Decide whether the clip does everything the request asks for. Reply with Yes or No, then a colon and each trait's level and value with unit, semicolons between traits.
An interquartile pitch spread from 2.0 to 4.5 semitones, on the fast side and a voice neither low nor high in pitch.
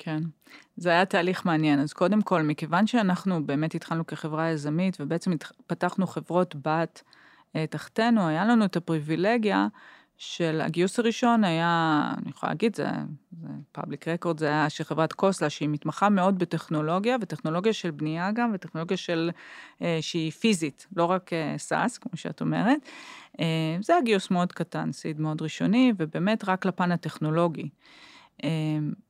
Yes: average, 3.3 semitones; fast, 155 wpm; medium, 170 Hz